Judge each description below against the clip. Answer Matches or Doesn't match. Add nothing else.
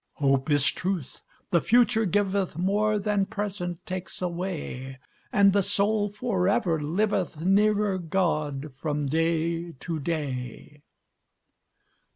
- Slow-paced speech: Matches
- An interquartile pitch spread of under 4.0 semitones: Doesn't match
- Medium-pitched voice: Matches